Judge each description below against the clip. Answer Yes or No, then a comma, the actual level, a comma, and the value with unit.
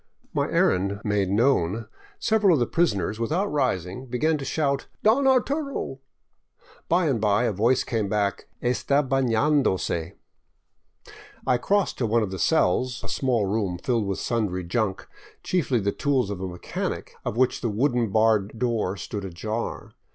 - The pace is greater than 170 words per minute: No, average, 165 wpm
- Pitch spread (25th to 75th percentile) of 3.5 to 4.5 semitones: No, wide, 5.5 semitones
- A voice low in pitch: Yes, low, 115 Hz